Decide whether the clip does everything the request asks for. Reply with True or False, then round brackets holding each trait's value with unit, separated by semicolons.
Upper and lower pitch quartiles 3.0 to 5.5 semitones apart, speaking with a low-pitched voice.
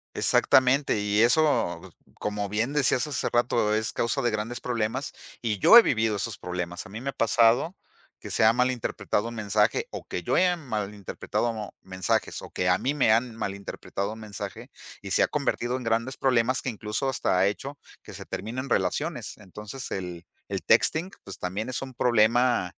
True (3.6 semitones; 115 Hz)